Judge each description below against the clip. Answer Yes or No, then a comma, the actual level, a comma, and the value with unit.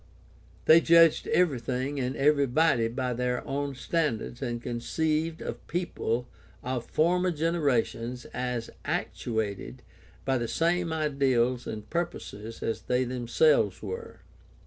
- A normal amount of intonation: Yes, average, 5.0 semitones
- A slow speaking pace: Yes, slow, 125 wpm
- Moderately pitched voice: No, low, 130 Hz